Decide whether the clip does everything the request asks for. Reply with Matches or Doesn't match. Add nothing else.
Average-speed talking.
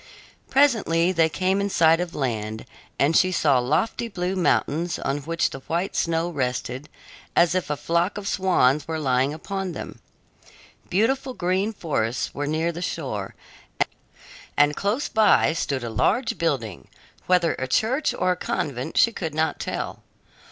Matches